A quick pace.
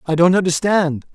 No: average, 155 wpm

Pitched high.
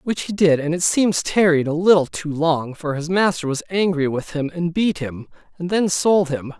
No: medium, 165 Hz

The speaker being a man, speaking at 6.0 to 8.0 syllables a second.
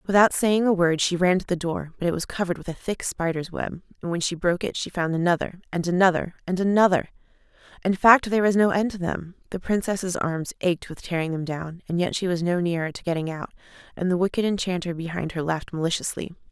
No: female; 6.1 syllables/s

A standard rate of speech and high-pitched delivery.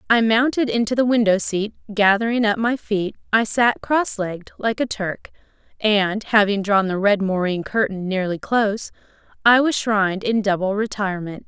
Yes: average, 165 wpm; high, 210 Hz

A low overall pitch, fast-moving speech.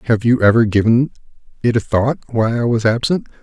No: low, 115 Hz; average, 195 wpm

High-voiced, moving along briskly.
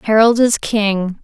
No: high, 215 Hz; average, 145 wpm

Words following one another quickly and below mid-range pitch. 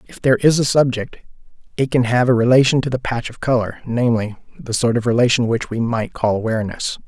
Yes: fast, 210 wpm; low, 120 Hz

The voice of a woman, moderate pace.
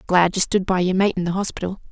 No: female; fast, 280 wpm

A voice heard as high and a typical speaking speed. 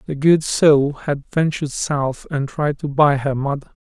No: medium, 145 Hz; average, 190 wpm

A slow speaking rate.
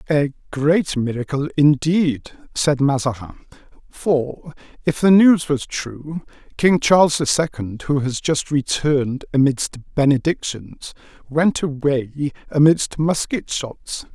Yes: slow, 115 wpm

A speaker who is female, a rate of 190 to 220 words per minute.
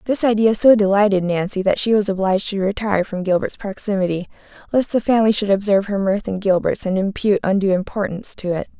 Yes: female; average, 200 wpm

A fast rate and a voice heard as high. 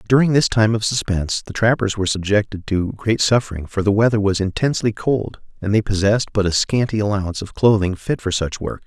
No: fast, 210 wpm; low, 105 Hz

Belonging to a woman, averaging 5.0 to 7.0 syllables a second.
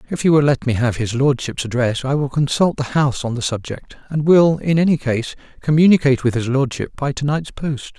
No: male; 5.5 syllables/s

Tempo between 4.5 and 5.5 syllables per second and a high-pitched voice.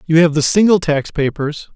No: 5.0 syllables/s; medium, 160 Hz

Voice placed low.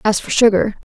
No: high, 210 Hz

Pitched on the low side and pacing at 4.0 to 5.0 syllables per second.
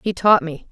No: medium, 180 Hz; 4.6 syllables/s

